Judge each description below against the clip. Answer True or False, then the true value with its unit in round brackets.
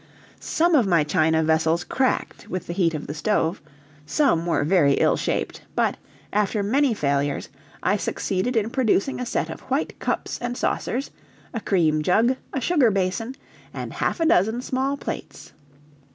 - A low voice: False (200 Hz)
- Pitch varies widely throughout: True (7.5 semitones)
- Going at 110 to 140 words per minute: False (165 wpm)